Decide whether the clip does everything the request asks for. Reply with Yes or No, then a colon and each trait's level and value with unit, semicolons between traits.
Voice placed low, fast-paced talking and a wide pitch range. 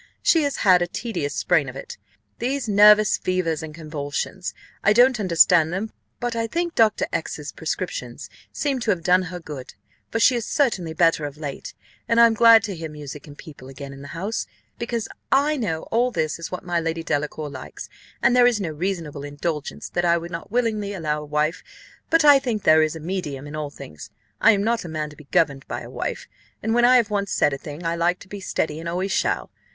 No: medium, 175 Hz; fast, 225 wpm; wide, 6.6 semitones